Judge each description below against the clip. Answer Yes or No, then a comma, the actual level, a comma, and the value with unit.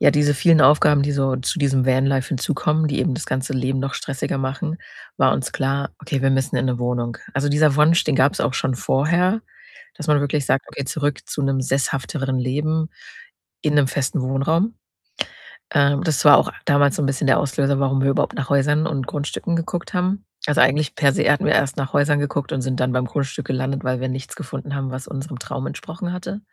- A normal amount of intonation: No, narrow, 2.1 semitones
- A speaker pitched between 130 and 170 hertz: Yes, medium, 140 Hz